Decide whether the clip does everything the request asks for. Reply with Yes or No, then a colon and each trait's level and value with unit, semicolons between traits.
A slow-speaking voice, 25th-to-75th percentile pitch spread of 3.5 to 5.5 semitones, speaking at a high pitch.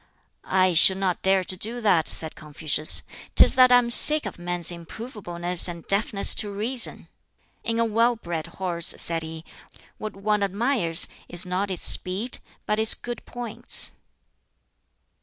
No: average, 150 wpm; average, 4.7 semitones; high, 195 Hz